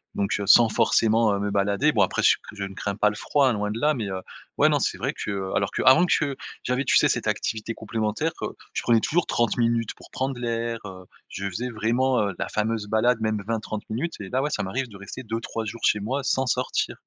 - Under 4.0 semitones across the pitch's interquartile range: Yes, average, 3.5 semitones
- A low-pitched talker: Yes, low, 115 Hz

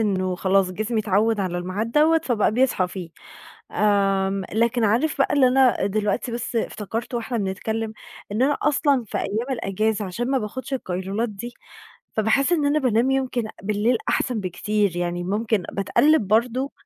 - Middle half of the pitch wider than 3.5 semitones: Yes, average, 4.1 semitones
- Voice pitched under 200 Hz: No, high, 220 Hz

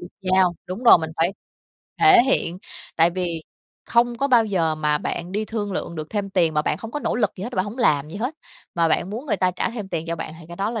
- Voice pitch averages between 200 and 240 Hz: No, medium, 185 Hz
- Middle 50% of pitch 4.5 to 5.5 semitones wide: Yes, average, 5.1 semitones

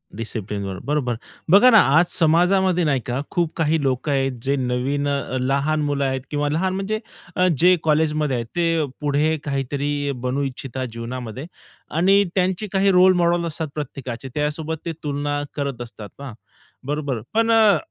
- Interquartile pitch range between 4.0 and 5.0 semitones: Yes, average, 4.3 semitones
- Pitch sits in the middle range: Yes, medium, 145 Hz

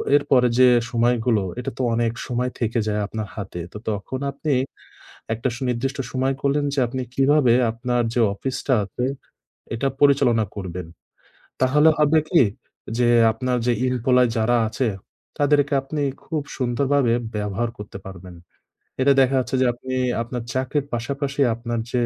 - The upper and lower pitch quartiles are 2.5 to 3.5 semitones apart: Yes, average, 2.9 semitones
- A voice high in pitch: No, low, 125 Hz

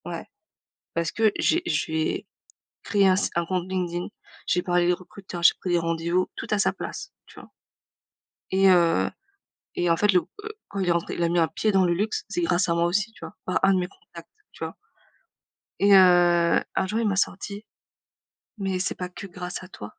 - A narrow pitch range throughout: Yes, narrow, 2.3 semitones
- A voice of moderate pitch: Yes, medium, 180 Hz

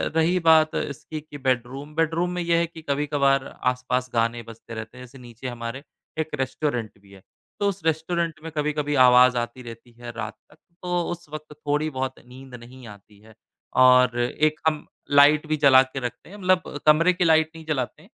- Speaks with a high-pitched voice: No, medium, 140 Hz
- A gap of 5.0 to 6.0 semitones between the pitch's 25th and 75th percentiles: No, average, 4.2 semitones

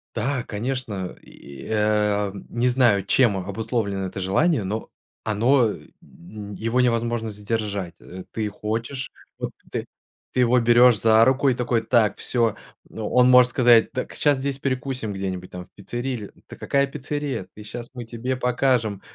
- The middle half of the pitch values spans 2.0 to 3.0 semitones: No, average, 3.4 semitones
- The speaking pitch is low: Yes, low, 115 Hz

